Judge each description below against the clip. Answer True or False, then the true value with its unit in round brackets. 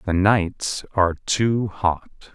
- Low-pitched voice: True (100 Hz)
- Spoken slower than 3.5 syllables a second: True (2.8 syllables/s)